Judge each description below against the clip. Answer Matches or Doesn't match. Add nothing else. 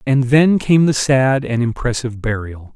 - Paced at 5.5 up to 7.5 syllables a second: Doesn't match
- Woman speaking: Doesn't match